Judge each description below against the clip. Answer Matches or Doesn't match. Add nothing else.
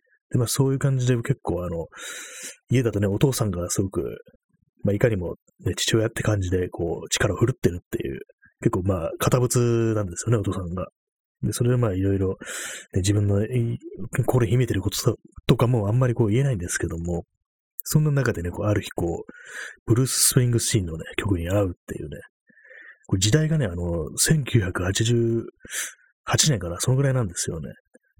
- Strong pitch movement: Doesn't match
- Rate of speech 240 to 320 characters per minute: Doesn't match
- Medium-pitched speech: Doesn't match